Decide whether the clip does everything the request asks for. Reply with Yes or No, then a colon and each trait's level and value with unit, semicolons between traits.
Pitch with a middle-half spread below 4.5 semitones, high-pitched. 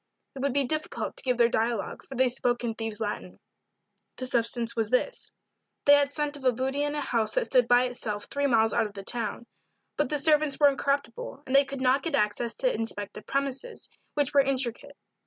Yes: average, 3.5 semitones; very high, 255 Hz